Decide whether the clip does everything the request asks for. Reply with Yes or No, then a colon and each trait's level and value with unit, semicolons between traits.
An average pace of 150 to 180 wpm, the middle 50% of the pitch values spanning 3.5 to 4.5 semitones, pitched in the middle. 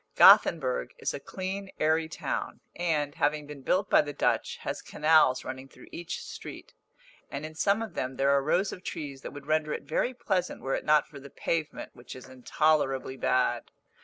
No: average, 190 wpm; average, 3.9 semitones; medium, 150 Hz